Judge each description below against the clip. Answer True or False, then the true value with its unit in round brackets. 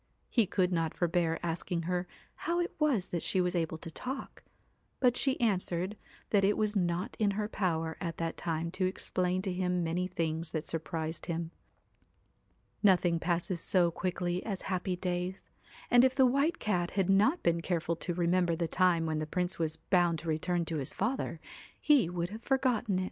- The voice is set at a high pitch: False (180 Hz)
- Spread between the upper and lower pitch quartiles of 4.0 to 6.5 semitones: False (2.9 semitones)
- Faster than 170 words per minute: True (190 wpm)